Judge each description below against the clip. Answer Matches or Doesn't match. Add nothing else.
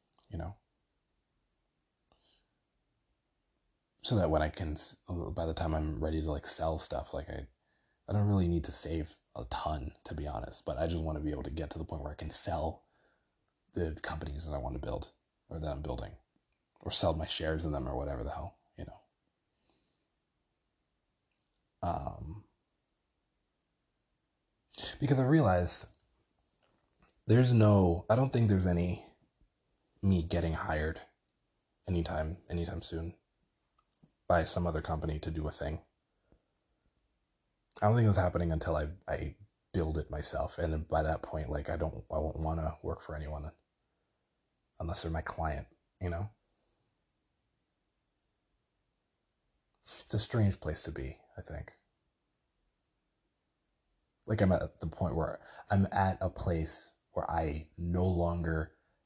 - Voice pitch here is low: Matches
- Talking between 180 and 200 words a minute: Doesn't match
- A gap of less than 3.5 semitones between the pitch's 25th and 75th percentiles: Matches